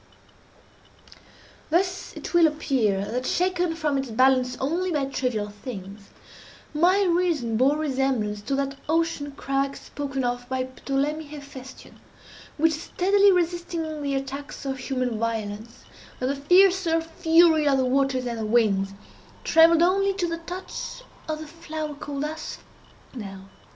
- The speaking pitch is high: Yes, very high, 280 Hz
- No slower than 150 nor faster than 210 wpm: No, slow, 135 wpm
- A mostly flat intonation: No, average, 4.5 semitones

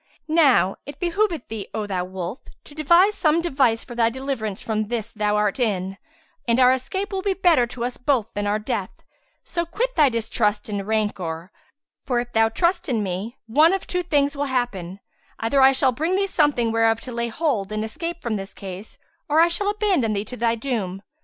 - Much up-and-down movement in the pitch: Yes, wide, 6.4 semitones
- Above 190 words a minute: Yes, fast, 205 wpm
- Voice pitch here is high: Yes, high, 240 Hz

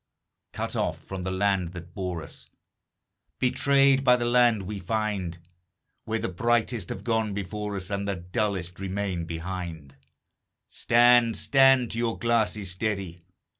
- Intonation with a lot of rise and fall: No, average, 4.3 semitones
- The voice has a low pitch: Yes, low, 100 Hz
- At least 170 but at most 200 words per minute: No, average, 140 wpm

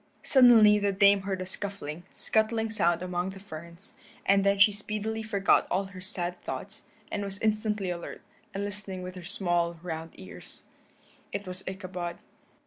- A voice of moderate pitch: No, high, 195 Hz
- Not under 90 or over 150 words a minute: No, average, 160 wpm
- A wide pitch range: No, narrow, 2.4 semitones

